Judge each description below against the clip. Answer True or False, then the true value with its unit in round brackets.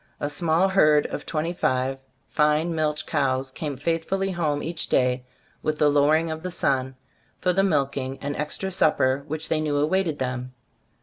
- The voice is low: False (150 Hz)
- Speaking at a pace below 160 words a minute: False (170 wpm)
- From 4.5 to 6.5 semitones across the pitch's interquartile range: False (3.2 semitones)